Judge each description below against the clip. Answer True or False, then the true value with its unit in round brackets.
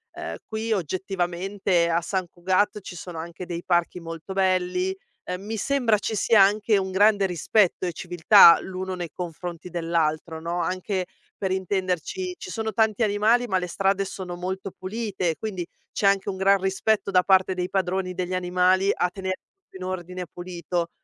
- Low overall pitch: False (185 Hz)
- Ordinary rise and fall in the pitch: False (1.9 semitones)